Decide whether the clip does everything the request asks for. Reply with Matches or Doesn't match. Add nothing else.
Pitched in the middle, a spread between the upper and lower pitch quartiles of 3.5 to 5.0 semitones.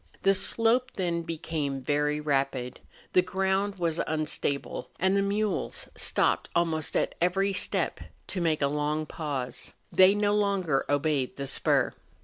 Matches